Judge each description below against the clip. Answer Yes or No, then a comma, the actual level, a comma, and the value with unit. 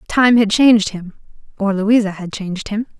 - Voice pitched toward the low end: No, high, 210 Hz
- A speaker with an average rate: Yes, average, 180 wpm